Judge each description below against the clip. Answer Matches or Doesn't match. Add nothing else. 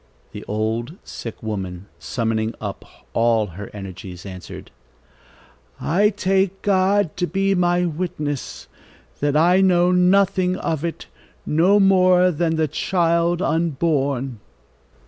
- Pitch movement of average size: Doesn't match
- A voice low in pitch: Doesn't match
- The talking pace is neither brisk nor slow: Doesn't match